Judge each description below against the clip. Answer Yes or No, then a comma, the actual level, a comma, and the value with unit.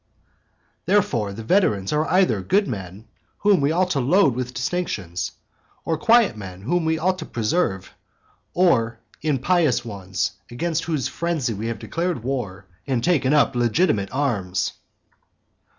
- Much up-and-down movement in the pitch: Yes, wide, 8.1 semitones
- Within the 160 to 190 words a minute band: No, average, 140 wpm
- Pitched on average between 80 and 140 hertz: Yes, low, 135 Hz